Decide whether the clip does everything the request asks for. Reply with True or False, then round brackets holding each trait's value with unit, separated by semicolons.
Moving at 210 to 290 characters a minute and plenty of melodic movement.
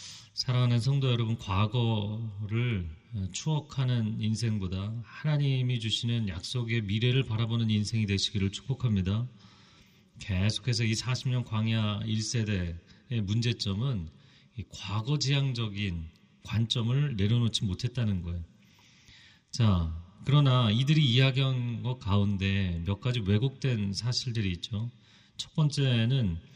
False (260 characters per minute; 3.6 semitones)